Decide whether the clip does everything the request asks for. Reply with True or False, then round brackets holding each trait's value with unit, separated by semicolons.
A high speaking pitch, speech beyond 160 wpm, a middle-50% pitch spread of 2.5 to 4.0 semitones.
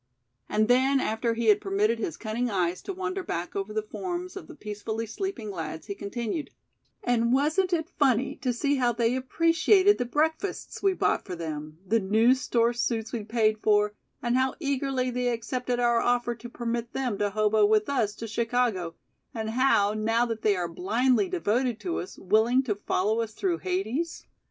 True (235 Hz; 185 wpm; 3.6 semitones)